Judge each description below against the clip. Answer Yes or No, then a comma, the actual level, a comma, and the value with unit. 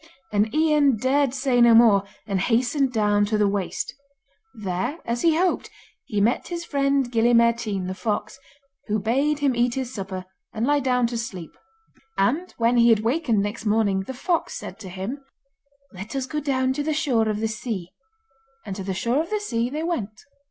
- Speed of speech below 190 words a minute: No, average, 195 wpm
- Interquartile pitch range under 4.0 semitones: No, average, 4.8 semitones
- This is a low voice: No, high, 235 Hz